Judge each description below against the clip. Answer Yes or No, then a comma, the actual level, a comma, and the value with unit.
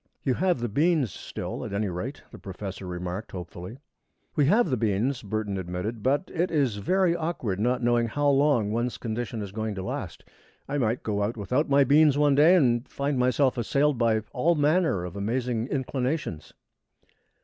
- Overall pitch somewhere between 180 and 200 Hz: No, low, 120 Hz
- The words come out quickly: No, average, 180 wpm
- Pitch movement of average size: No, wide, 5.7 semitones